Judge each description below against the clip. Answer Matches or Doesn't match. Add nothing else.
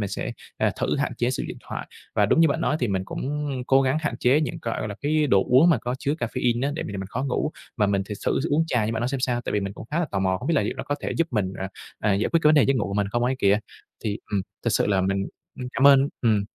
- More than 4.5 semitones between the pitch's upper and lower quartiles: Matches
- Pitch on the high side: Doesn't match